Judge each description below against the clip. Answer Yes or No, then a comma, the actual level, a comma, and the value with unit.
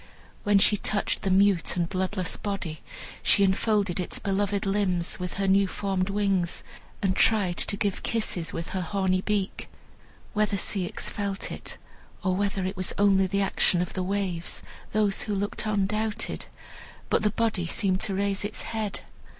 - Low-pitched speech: No, high, 195 Hz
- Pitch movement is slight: Yes, narrow, 1.6 semitones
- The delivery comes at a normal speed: Yes, average, 165 wpm